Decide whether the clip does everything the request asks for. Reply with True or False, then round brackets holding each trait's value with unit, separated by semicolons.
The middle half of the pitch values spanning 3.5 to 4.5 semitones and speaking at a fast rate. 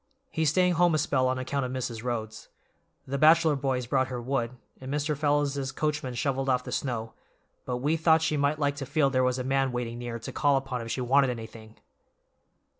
False (2.7 semitones; 210 wpm)